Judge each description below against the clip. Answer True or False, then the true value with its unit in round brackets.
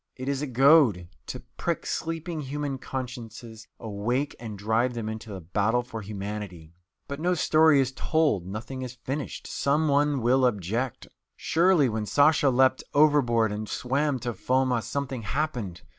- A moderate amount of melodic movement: True (4.5 semitones)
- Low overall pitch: True (125 Hz)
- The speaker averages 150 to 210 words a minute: True (155 wpm)